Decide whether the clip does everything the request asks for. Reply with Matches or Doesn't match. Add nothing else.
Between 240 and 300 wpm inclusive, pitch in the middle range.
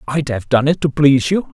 Matches